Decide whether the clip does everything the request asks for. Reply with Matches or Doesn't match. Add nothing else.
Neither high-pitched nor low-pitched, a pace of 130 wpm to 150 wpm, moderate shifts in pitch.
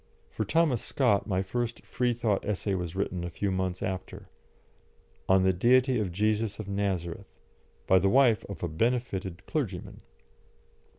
Doesn't match